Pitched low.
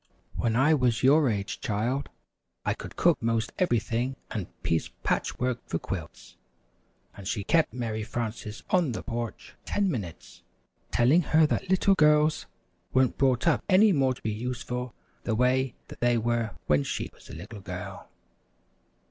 Yes: low, 120 Hz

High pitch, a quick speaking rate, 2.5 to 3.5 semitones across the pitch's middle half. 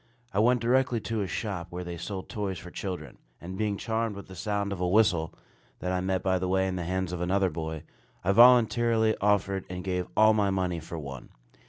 No: very low, 95 Hz; fast, 220 wpm; average, 3.0 semitones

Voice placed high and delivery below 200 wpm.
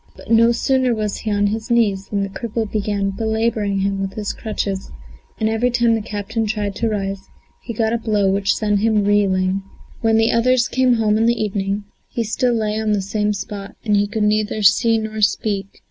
No: high, 215 Hz; fast, 205 wpm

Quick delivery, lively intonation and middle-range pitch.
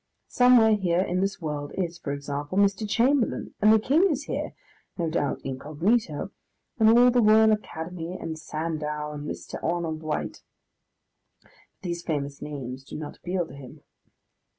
No: average, 155 wpm; wide, 6.2 semitones; medium, 170 Hz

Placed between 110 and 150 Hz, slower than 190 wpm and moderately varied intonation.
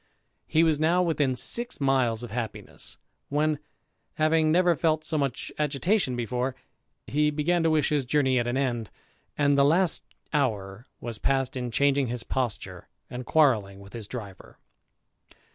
Yes: medium, 140 Hz; average, 155 wpm; average, 4.3 semitones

